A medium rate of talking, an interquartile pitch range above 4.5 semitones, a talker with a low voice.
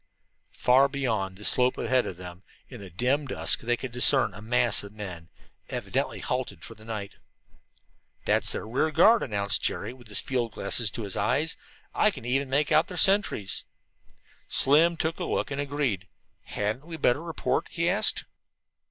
Yes: average, 175 wpm; wide, 5.6 semitones; low, 125 Hz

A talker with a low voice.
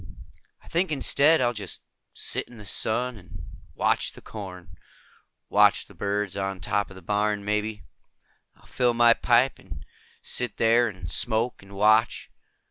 Yes: low, 105 Hz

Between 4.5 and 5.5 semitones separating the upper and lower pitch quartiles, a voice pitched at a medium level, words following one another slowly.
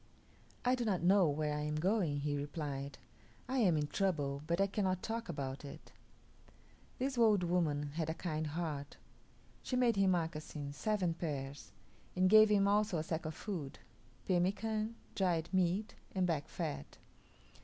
No: average, 5.1 semitones; medium, 170 Hz; average, 160 wpm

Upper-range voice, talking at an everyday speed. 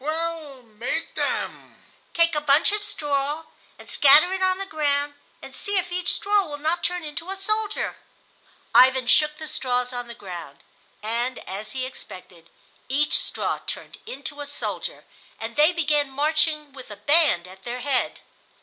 Yes: very high, 290 Hz; average, 165 wpm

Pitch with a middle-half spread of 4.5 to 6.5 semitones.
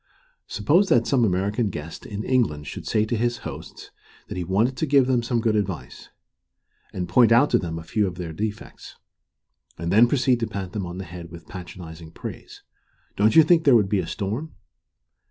Yes: average, 5.2 semitones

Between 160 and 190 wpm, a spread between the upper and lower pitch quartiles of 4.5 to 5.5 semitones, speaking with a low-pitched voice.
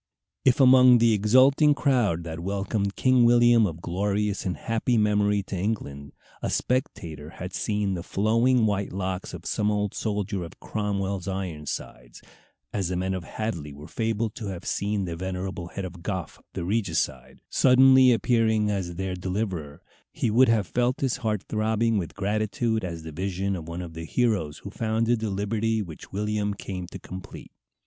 No: average, 170 wpm; average, 3.6 semitones; low, 100 Hz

